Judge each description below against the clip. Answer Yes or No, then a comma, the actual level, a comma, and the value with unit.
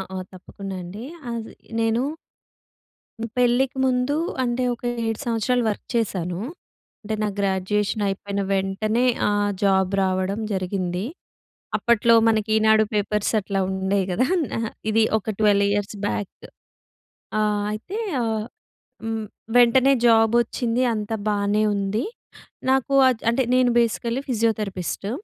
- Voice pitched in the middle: No, high, 215 Hz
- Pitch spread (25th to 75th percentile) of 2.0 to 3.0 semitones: Yes, average, 2.7 semitones